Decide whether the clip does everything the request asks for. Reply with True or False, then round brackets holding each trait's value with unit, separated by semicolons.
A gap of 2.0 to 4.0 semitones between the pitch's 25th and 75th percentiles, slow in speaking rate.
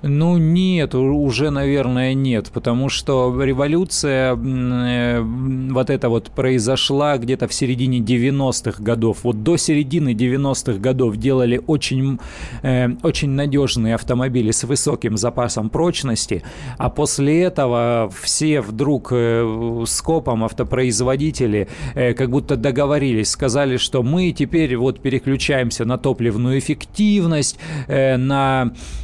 False (2.7 semitones; 120 wpm)